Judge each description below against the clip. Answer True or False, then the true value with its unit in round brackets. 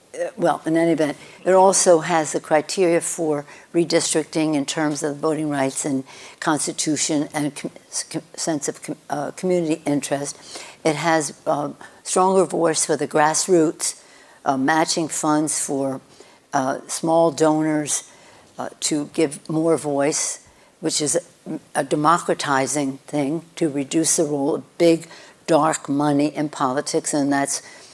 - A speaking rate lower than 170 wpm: True (140 wpm)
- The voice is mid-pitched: True (155 Hz)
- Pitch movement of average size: False (2.2 semitones)